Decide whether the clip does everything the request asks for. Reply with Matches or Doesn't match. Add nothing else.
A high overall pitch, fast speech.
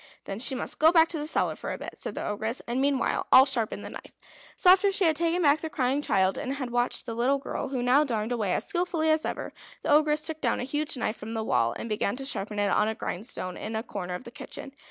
Matches